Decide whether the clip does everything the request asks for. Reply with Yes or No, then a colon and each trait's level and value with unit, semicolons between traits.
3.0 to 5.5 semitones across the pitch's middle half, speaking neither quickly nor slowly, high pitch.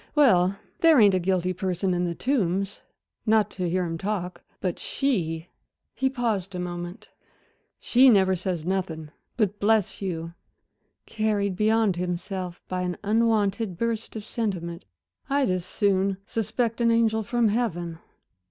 Yes: average, 3.8 semitones; average, 145 wpm; high, 195 Hz